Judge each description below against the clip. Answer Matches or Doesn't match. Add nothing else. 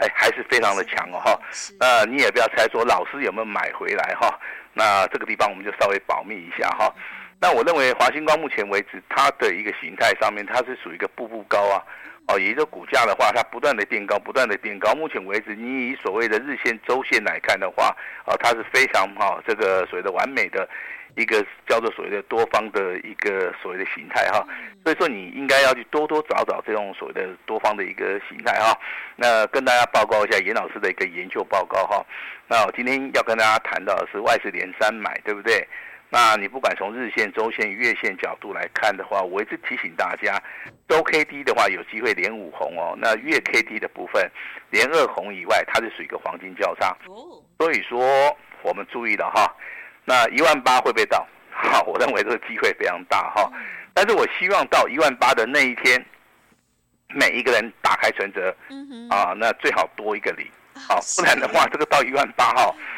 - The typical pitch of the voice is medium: Matches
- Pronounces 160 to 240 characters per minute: Doesn't match